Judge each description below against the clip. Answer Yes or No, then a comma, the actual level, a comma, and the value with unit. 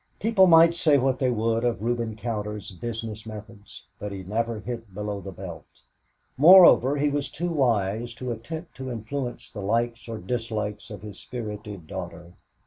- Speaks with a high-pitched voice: No, low, 115 Hz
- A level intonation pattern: No, average, 3.6 semitones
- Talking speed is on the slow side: No, average, 165 wpm